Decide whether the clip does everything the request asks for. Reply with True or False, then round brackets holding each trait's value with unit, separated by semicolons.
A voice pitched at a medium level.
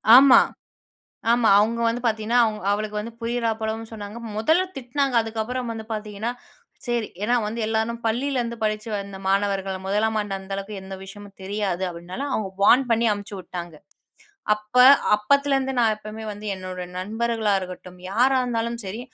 False (220 Hz)